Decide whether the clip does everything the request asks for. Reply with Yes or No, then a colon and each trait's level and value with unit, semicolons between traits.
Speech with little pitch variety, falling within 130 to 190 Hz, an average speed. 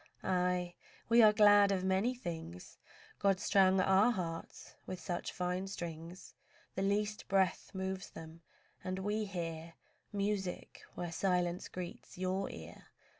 No: narrow, 2.2 semitones; medium, 185 Hz; slow, 130 wpm